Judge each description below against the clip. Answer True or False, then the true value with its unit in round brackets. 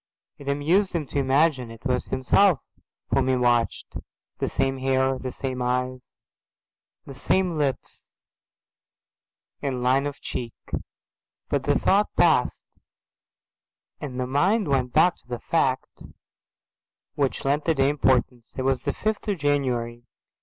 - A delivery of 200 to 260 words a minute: False (140 wpm)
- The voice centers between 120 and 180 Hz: True (135 Hz)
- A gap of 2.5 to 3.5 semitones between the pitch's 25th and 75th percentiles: True (2.8 semitones)